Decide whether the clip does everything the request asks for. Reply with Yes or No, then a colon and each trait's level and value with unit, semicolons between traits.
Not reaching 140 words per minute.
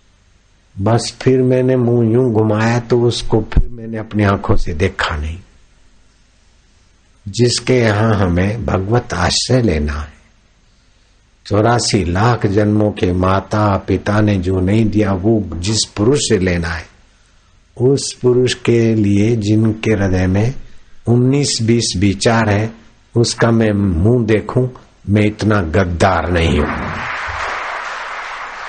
Yes: average, 120 wpm